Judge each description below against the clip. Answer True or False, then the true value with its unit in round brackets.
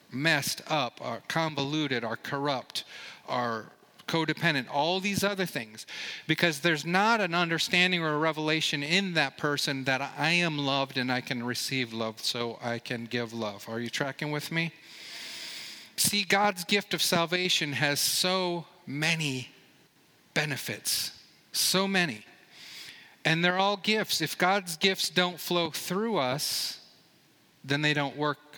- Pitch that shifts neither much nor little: True (4.5 semitones)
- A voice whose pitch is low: False (155 Hz)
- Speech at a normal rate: True (145 wpm)